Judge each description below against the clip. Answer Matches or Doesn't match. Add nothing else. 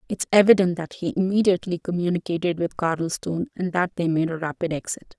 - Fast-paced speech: Doesn't match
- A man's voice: Doesn't match